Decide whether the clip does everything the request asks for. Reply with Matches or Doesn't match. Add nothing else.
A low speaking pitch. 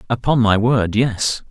Matches